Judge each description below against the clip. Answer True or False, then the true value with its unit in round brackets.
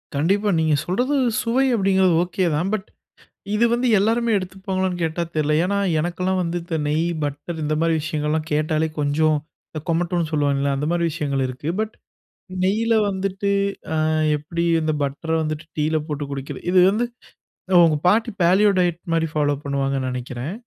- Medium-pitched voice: True (165 Hz)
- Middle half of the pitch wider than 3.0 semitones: True (4.0 semitones)